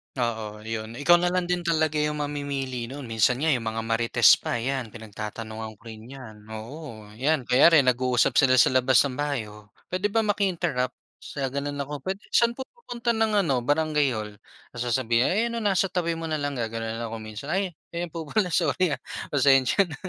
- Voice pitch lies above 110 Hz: Yes, medium, 140 Hz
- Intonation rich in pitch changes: Yes, wide, 6.4 semitones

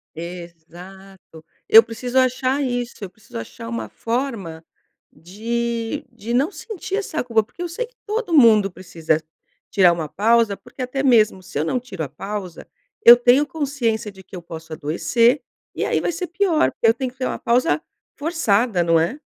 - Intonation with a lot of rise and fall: Yes, wide, 6.5 semitones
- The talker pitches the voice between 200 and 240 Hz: Yes, high, 230 Hz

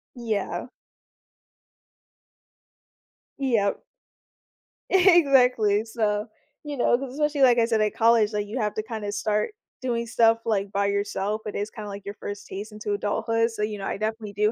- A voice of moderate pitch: No, high, 215 Hz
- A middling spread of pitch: No, narrow, 2.3 semitones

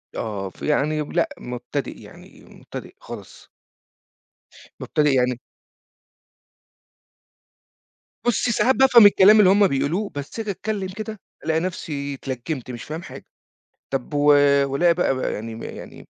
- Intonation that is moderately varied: No, wide, 6.7 semitones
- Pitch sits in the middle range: Yes, medium, 155 Hz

